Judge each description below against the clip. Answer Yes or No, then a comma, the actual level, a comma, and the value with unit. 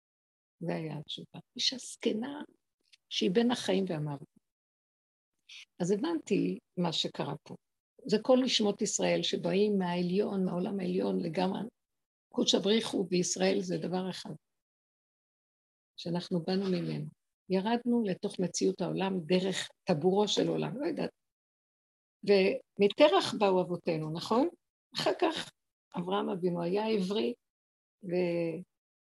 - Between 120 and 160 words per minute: No, average, 110 wpm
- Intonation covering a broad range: No, average, 3.5 semitones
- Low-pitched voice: No, high, 190 Hz